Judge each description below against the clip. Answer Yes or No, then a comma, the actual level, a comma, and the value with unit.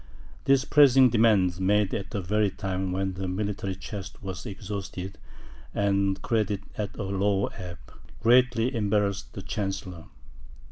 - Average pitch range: No, narrow, 2.0 semitones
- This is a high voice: No, low, 100 Hz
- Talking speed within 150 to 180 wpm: No, slow, 135 wpm